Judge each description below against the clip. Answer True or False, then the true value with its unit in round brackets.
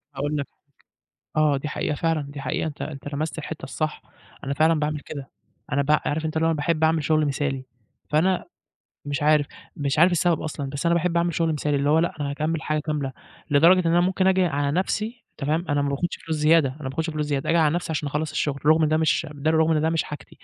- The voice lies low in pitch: False (155 Hz)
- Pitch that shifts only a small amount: True (2.1 semitones)